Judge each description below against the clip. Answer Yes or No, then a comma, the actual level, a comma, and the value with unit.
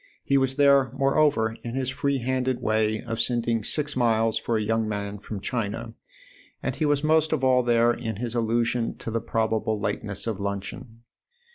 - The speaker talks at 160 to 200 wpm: Yes, average, 180 wpm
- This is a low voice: Yes, low, 115 Hz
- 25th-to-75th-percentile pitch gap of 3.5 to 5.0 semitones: No, average, 3.0 semitones